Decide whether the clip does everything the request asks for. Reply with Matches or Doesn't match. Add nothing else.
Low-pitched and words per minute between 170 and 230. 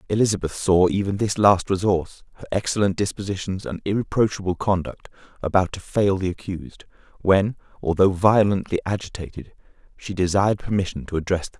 Doesn't match